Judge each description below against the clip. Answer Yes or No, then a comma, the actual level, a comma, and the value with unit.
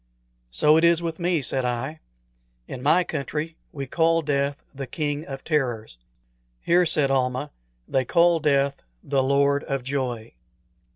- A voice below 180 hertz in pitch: Yes, medium, 140 Hz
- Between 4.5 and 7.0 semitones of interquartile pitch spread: No, average, 3.3 semitones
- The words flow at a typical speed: Yes, average, 150 wpm